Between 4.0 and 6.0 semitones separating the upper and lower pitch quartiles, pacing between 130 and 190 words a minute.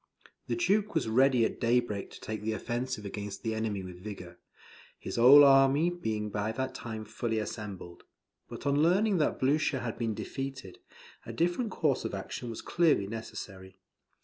Yes: average, 4.9 semitones; average, 170 wpm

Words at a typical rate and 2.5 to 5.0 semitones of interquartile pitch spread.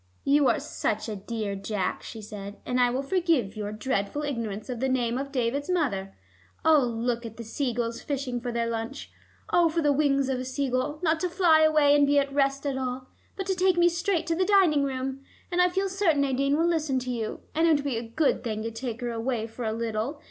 No: fast, 240 wpm; average, 4.7 semitones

